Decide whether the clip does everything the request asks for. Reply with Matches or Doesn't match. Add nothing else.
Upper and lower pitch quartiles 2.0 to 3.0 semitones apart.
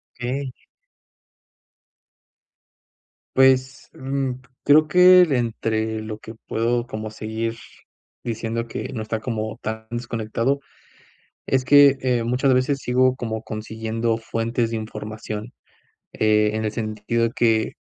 Matches